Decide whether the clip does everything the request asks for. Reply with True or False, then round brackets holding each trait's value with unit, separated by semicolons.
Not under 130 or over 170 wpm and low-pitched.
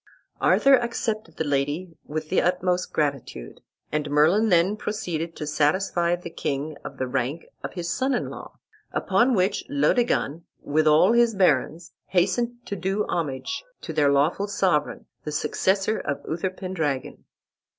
False (150 wpm; 175 Hz)